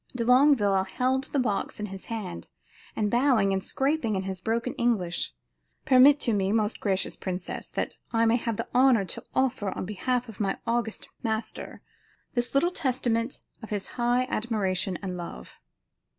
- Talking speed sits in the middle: Yes, average, 165 wpm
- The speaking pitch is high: Yes, high, 225 Hz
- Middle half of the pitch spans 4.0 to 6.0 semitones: Yes, average, 4.3 semitones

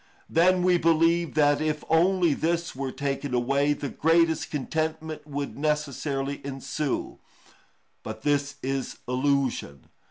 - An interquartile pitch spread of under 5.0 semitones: Yes, average, 2.8 semitones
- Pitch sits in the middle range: Yes, medium, 145 Hz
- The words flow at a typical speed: No, slow, 120 wpm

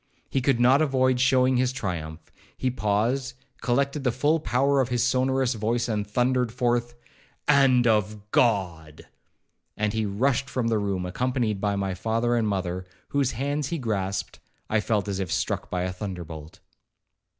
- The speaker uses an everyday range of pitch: Yes, average, 4.4 semitones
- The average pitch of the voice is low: Yes, low, 120 Hz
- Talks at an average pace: Yes, average, 165 wpm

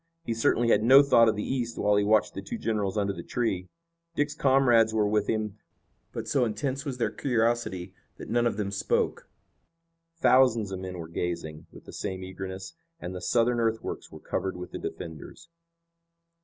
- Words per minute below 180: No, average, 185 wpm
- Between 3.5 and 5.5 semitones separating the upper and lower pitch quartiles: Yes, average, 4.0 semitones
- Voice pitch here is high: No, low, 110 Hz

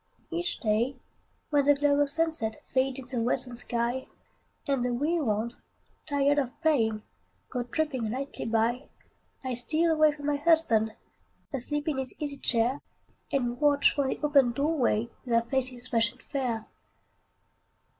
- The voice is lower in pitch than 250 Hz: No, very high, 265 Hz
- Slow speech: No, average, 155 wpm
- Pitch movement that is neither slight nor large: Yes, average, 3.4 semitones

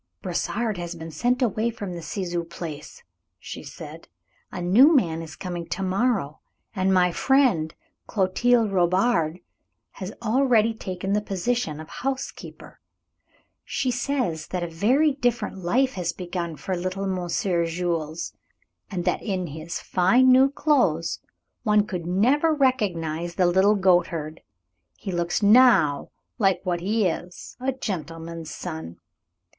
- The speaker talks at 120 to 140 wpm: Yes, slow, 135 wpm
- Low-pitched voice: No, medium, 185 Hz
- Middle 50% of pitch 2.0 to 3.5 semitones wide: No, wide, 5.5 semitones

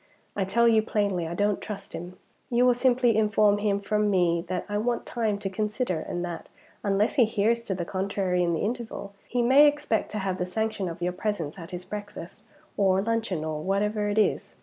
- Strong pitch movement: No, average, 3.3 semitones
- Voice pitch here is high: Yes, high, 205 Hz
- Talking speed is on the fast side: Yes, fast, 210 wpm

